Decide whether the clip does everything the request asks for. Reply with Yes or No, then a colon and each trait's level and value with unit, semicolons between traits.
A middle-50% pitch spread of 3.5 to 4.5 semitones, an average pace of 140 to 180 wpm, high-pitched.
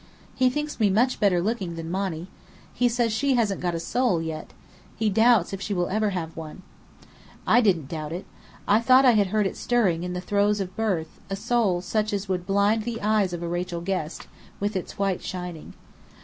No: average, 3.8 semitones; fast, 205 wpm; high, 195 Hz